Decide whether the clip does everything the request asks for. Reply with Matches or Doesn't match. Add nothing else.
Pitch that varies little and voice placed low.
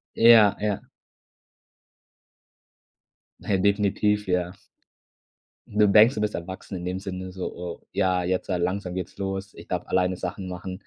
Matches